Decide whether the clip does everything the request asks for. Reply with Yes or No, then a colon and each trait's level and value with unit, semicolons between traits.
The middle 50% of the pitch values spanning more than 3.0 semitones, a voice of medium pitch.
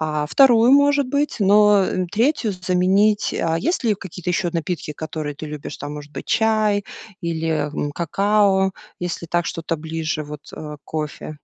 Yes: average, 5.1 semitones; medium, 180 Hz